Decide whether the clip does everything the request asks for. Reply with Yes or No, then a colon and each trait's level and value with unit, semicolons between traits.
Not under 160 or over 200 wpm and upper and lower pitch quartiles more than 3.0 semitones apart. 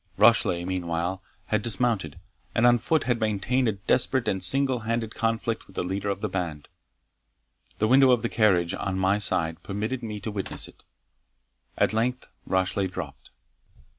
Yes: average, 165 wpm; average, 3.8 semitones